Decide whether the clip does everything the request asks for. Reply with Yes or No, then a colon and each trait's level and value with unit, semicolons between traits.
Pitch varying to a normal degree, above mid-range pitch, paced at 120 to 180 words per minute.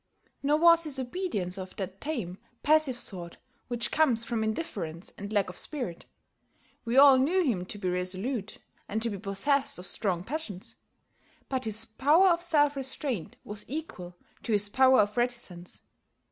No: wide, 6.6 semitones; high, 235 Hz; average, 160 wpm